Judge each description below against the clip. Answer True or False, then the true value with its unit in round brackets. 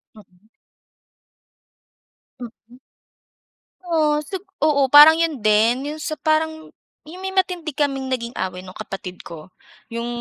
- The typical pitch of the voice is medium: False (275 Hz)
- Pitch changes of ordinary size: False (6.4 semitones)